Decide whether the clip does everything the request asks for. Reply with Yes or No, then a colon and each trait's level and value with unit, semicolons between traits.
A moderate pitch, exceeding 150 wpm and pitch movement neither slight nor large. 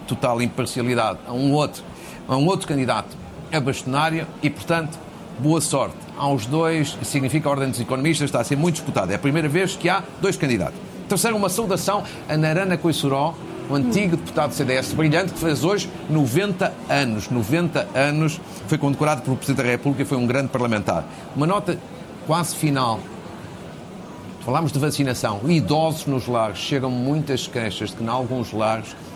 Yes: medium, 145 Hz; average, 175 wpm; average, 4.1 semitones